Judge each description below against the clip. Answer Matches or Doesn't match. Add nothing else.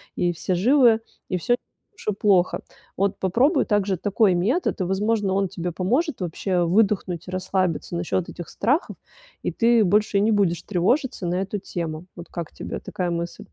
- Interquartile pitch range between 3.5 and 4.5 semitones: Matches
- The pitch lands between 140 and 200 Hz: Matches